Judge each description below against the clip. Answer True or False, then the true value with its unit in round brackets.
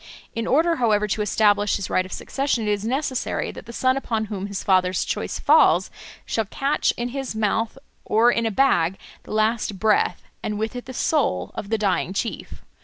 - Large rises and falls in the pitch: False (3.3 semitones)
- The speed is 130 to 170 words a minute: False (195 wpm)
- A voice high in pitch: True (220 Hz)